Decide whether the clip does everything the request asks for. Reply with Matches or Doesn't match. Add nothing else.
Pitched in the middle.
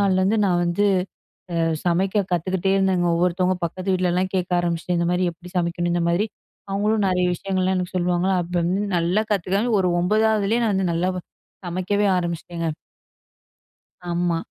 Matches